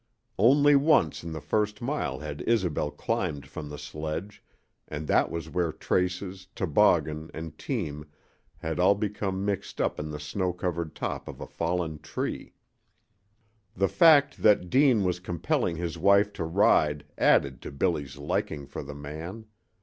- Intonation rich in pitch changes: No, average, 4.8 semitones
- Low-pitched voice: Yes, very low, 85 Hz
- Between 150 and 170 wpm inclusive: Yes, average, 155 wpm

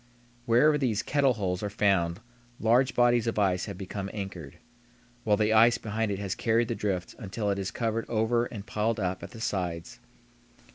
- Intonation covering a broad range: No, average, 3.0 semitones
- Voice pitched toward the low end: Yes, low, 105 Hz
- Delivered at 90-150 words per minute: No, average, 185 wpm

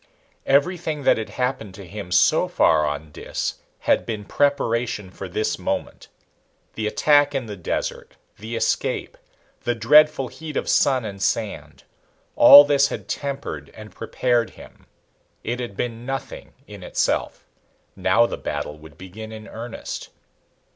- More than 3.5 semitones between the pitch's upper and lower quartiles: Yes, average, 5.3 semitones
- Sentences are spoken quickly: No, average, 145 wpm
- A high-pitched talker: No, low, 115 Hz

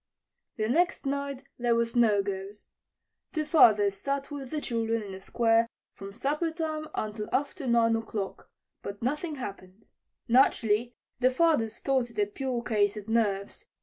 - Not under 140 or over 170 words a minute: Yes, average, 155 wpm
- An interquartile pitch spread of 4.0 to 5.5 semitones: Yes, average, 4.8 semitones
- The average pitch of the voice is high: Yes, high, 235 Hz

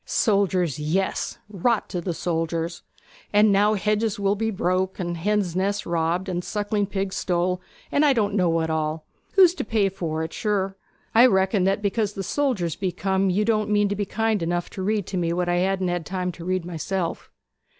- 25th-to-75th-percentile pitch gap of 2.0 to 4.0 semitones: Yes, average, 3.0 semitones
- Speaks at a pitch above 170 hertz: Yes, high, 190 Hz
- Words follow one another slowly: No, average, 190 wpm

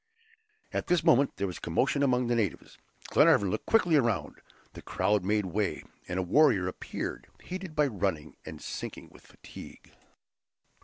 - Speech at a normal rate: Yes, average, 160 wpm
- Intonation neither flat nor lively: No, wide, 7.1 semitones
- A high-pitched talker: No, low, 110 Hz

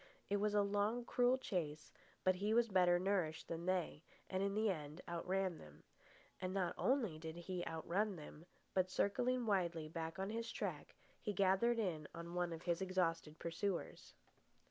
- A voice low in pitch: No, medium, 185 Hz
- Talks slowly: No, average, 165 wpm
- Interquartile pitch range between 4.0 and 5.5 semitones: No, average, 3.5 semitones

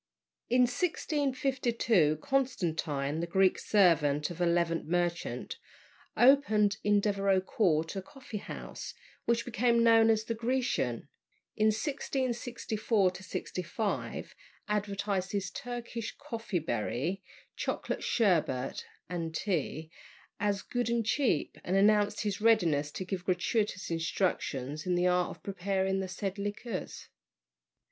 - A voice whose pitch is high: Yes, high, 200 Hz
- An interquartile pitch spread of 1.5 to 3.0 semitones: No, average, 4.7 semitones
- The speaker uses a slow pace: Yes, slow, 120 wpm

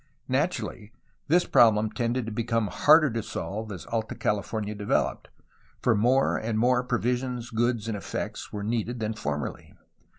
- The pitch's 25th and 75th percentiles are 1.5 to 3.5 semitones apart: Yes, narrow, 2.4 semitones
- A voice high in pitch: No, low, 115 Hz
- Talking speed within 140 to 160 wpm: Yes, average, 155 wpm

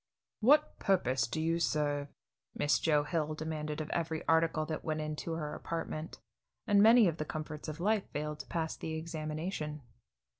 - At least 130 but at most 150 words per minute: No, average, 165 wpm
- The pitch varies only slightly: Yes, narrow, 1.6 semitones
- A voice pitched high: No, medium, 155 Hz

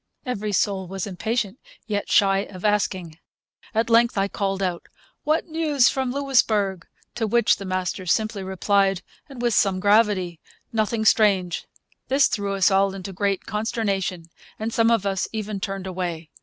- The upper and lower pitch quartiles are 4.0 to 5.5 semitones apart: No, average, 2.9 semitones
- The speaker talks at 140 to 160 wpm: Yes, average, 155 wpm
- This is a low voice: No, high, 200 Hz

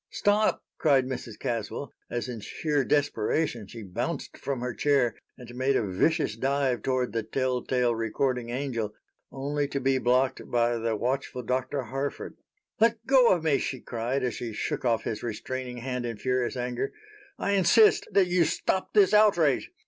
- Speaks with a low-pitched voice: Yes, low, 130 Hz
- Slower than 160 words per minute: No, average, 170 wpm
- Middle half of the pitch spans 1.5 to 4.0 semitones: Yes, average, 3.2 semitones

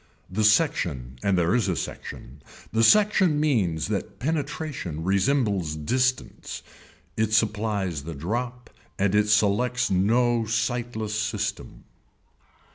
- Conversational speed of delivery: No, slow, 115 wpm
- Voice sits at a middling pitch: No, low, 110 Hz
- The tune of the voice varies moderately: Yes, average, 4.7 semitones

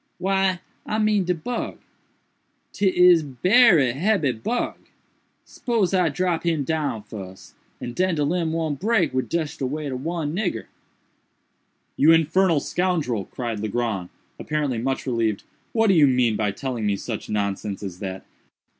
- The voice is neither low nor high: Yes, medium, 150 Hz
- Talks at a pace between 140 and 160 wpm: Yes, average, 150 wpm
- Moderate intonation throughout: No, wide, 7.2 semitones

